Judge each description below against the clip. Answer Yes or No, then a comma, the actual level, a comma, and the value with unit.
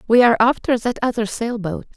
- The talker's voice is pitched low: No, high, 230 Hz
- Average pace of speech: No, fast, 215 wpm